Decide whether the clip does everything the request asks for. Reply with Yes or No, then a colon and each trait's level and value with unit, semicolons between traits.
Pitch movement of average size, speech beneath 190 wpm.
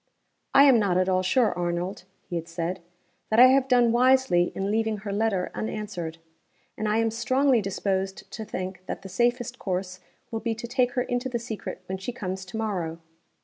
No: average, 4.5 semitones; average, 195 wpm